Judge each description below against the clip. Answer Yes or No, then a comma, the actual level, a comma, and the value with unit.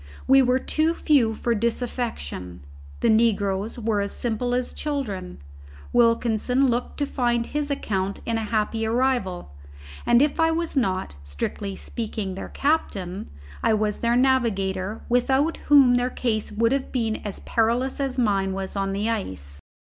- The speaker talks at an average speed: Yes, average, 155 wpm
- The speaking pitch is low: No, high, 230 Hz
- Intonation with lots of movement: No, average, 4.2 semitones